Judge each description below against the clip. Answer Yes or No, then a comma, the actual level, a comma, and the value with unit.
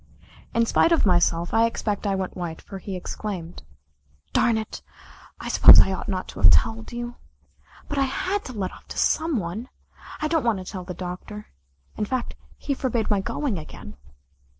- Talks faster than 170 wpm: Yes, average, 190 wpm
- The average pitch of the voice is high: Yes, high, 205 Hz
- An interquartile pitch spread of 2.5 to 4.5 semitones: No, average, 5.0 semitones